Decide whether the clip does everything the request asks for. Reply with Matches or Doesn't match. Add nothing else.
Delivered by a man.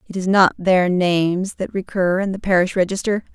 Doesn't match